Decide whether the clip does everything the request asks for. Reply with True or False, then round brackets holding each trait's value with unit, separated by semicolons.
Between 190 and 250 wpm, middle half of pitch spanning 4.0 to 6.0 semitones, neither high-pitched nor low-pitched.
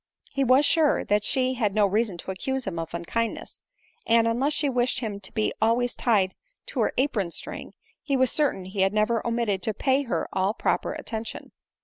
False (200 wpm; 4.4 semitones; 230 Hz)